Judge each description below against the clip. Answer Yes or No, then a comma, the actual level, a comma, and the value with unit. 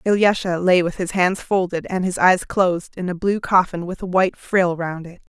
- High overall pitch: No, medium, 180 Hz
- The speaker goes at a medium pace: No, fast, 225 wpm